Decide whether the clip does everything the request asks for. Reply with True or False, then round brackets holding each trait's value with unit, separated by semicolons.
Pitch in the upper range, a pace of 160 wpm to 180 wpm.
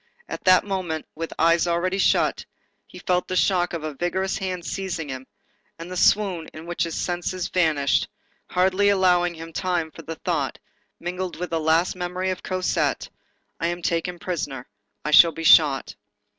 False (175 Hz; 170 wpm)